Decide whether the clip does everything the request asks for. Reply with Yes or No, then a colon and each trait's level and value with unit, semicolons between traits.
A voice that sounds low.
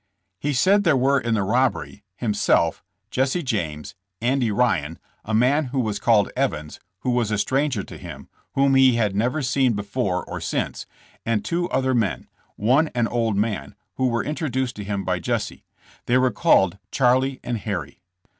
Yes: low, 120 Hz